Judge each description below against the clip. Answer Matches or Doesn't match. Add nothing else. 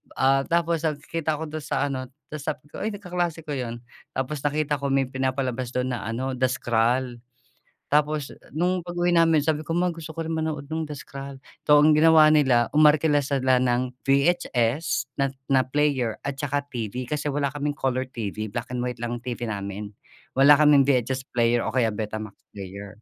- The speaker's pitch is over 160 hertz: Doesn't match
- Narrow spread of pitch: Doesn't match